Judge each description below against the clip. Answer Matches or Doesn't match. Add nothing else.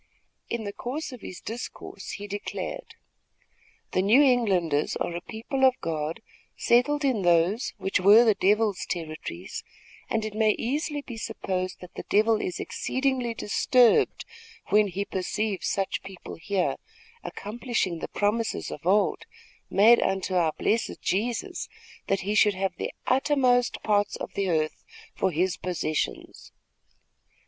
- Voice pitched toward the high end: Matches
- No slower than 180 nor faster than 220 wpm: Doesn't match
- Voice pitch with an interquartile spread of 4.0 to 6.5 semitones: Matches